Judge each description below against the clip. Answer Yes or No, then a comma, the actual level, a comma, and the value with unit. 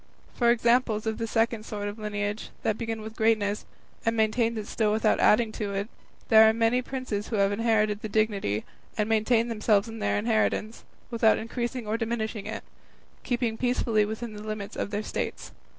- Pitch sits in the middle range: No, high, 220 Hz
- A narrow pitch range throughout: Yes, narrow, 1.4 semitones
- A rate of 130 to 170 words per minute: No, average, 185 wpm